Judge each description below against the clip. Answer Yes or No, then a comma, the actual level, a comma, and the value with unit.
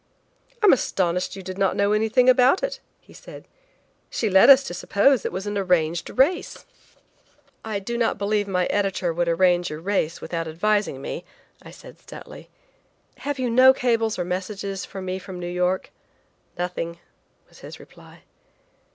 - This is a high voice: Yes, high, 195 Hz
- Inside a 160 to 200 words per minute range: Yes, average, 170 wpm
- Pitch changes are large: No, average, 4.1 semitones